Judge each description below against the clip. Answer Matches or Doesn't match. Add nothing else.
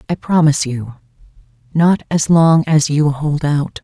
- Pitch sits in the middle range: Matches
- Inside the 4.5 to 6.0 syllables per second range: Doesn't match